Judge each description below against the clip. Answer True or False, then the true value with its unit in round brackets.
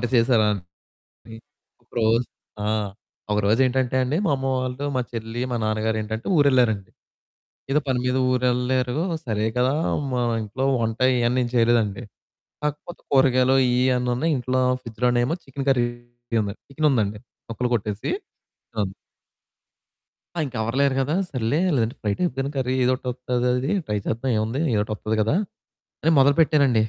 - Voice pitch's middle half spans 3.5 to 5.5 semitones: False (2.9 semitones)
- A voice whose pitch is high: False (125 Hz)